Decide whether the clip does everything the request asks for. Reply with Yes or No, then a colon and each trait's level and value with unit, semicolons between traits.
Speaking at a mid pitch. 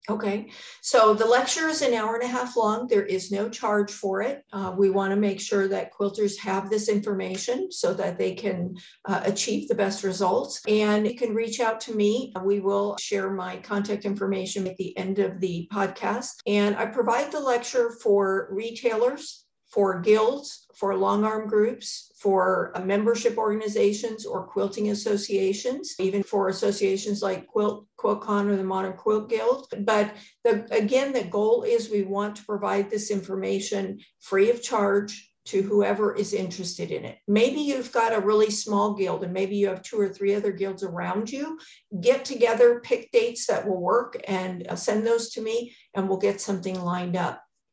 No: high, 210 Hz